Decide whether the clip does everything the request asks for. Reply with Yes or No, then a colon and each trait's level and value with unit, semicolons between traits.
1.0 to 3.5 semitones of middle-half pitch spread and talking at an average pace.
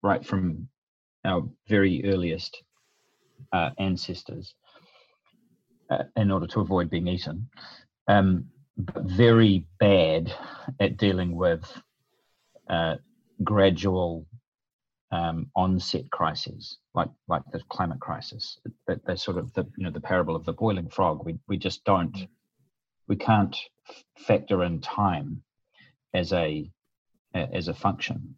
No: average, 3.0 semitones; slow, 120 wpm